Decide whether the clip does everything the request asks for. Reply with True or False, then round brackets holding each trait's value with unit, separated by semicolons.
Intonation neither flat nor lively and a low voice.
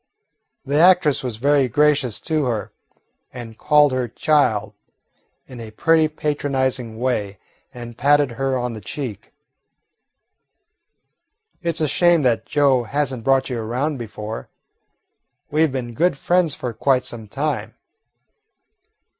True (3.9 semitones; 130 Hz)